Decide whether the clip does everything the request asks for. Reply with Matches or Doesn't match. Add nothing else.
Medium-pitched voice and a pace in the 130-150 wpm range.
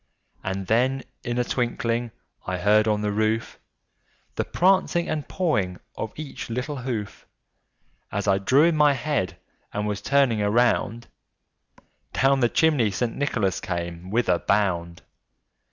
Doesn't match